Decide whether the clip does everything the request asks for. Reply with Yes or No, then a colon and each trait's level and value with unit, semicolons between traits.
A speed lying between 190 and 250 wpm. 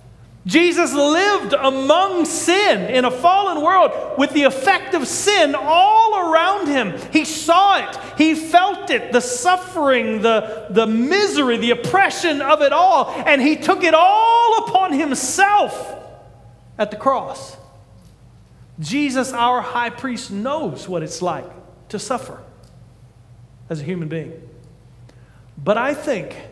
No: slow, 135 wpm